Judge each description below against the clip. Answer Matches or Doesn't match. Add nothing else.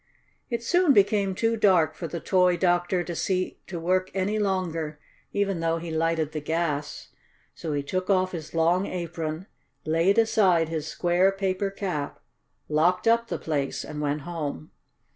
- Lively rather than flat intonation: Doesn't match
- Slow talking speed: Doesn't match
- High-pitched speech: Doesn't match